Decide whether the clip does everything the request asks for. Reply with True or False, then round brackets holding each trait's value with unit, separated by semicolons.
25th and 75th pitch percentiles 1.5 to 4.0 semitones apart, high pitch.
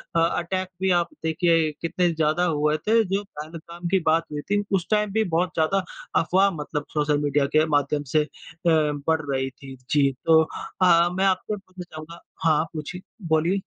False (3.3 semitones; 165 Hz)